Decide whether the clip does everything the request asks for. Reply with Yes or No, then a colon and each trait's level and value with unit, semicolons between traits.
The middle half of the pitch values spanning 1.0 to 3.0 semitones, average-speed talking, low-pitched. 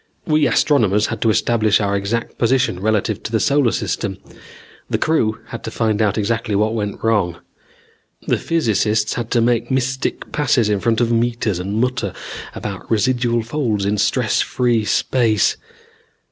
Yes: narrow, 2.5 semitones; average, 160 wpm; low, 115 Hz